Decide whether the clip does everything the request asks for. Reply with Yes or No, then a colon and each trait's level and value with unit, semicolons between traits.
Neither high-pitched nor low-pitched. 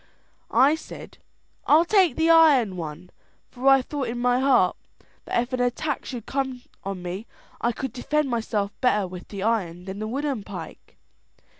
No: high, 245 Hz